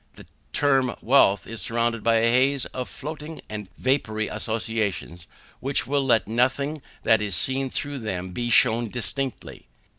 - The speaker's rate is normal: Yes, average, 150 wpm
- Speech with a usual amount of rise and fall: Yes, average, 3.7 semitones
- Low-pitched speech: Yes, low, 120 Hz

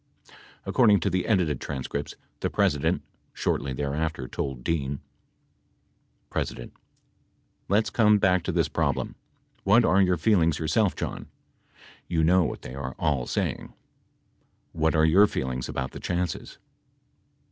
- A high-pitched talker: No, very low, 80 Hz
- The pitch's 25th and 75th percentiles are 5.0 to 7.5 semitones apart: Yes, wide, 5.4 semitones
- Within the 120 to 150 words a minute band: Yes, slow, 135 wpm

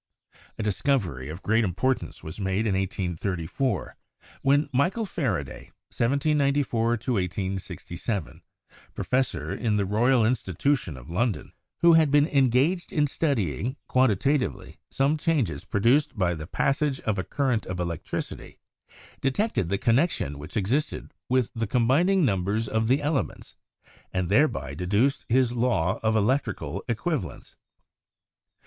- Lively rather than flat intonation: Yes, wide, 6.7 semitones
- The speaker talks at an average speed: No, slow, 125 wpm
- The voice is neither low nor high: No, low, 115 Hz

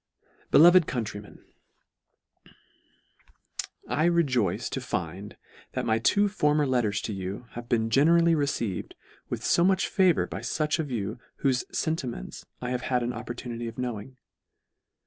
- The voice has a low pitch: Yes, low, 125 Hz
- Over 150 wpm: No, average, 140 wpm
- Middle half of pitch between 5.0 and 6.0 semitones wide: Yes, wide, 5.6 semitones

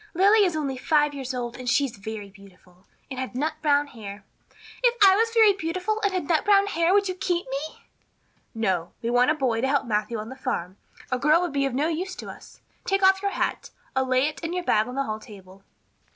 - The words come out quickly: Yes, fast, 240 wpm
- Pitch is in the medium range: No, very high, 275 Hz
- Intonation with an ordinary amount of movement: No, wide, 7.7 semitones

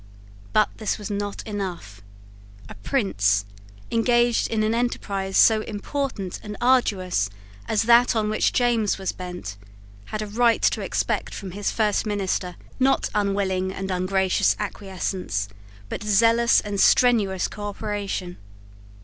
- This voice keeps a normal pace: No, slow, 130 wpm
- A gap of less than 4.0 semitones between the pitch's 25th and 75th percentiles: Yes, average, 2.9 semitones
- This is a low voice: No, high, 205 Hz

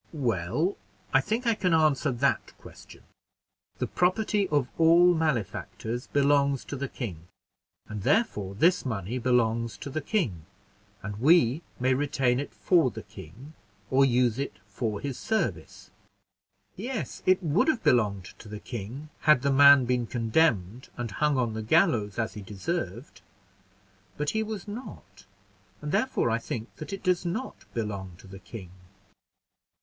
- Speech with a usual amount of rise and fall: No, wide, 6.7 semitones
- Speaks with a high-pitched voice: No, low, 130 Hz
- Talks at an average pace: Yes, average, 155 wpm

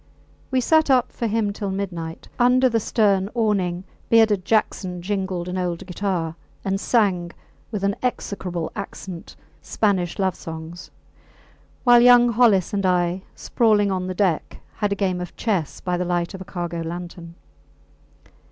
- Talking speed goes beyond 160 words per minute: No, average, 150 wpm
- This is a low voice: No, high, 190 Hz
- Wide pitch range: No, average, 3.5 semitones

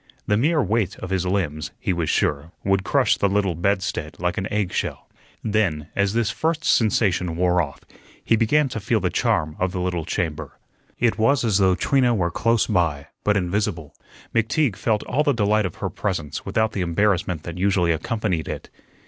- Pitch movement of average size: Yes, average, 4.1 semitones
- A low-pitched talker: Yes, very low, 95 Hz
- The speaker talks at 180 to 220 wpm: Yes, average, 190 wpm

